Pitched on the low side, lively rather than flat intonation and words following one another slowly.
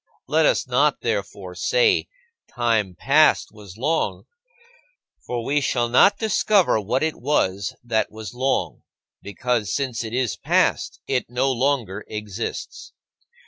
No: low, 120 Hz; average, 4.8 semitones; slow, 130 wpm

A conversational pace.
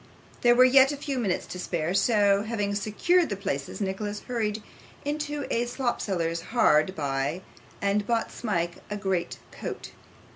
Yes: average, 150 wpm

